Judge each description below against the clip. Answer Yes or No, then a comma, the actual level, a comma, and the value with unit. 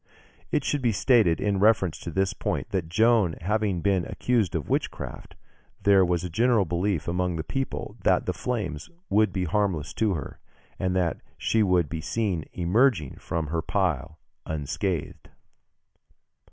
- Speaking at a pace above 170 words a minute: No, average, 155 wpm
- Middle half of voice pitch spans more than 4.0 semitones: Yes, average, 4.4 semitones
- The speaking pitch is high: No, very low, 95 Hz